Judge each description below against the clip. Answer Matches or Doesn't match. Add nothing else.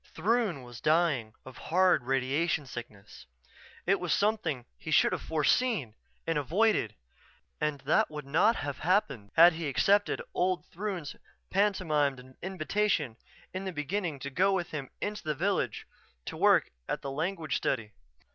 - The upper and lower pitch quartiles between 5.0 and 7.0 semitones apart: Matches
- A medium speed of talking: Matches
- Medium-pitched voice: Matches